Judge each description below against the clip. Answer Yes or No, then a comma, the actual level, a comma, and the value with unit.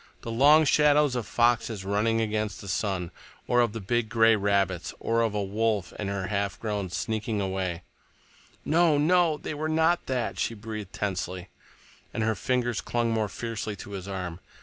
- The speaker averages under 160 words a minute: No, average, 175 wpm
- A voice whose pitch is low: Yes, low, 110 Hz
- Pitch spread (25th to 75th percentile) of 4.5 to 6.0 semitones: No, average, 3.3 semitones